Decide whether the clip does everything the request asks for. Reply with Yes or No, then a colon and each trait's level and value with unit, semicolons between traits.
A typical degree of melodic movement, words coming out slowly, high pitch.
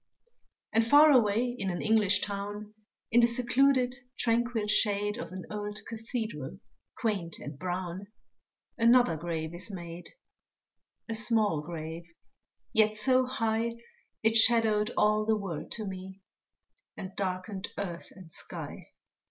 Yes: average, 3.6 semitones; slow, 125 wpm; high, 210 Hz